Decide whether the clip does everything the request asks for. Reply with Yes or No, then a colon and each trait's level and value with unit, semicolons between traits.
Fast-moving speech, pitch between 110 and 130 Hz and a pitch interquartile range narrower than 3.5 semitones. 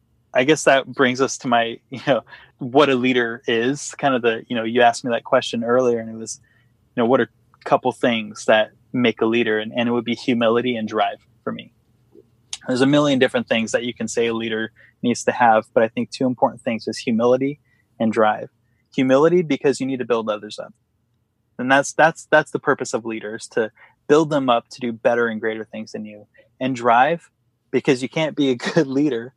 Yes: fast, 225 wpm; low, 120 Hz; average, 2.8 semitones